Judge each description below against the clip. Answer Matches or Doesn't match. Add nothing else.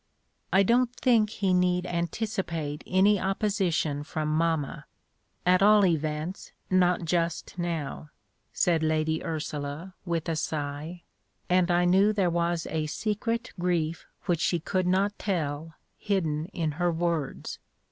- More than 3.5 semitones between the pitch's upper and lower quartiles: Doesn't match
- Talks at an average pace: Doesn't match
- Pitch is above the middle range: Doesn't match